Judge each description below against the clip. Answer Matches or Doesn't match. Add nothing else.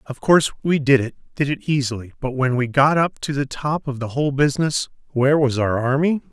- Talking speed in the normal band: Doesn't match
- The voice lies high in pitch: Doesn't match